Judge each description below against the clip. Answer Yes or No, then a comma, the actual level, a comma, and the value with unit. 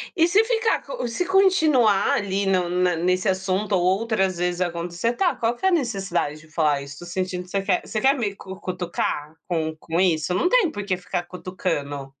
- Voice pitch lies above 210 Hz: No, medium, 185 Hz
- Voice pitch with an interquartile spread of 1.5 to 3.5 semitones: No, average, 4.8 semitones